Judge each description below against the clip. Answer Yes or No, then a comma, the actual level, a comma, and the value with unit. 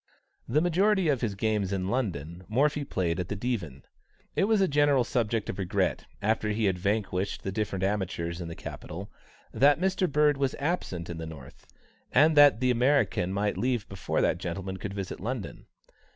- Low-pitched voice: Yes, low, 105 Hz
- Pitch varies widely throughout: Yes, wide, 6.9 semitones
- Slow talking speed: No, average, 180 wpm